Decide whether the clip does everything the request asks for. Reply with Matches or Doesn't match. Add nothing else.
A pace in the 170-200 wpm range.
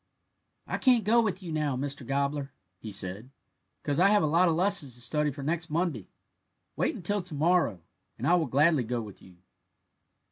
Matches